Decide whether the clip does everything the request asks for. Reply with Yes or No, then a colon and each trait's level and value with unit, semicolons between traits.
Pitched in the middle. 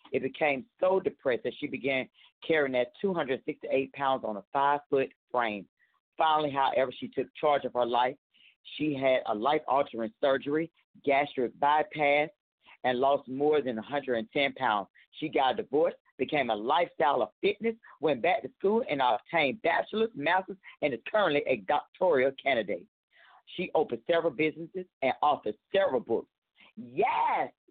Yes: medium, 145 Hz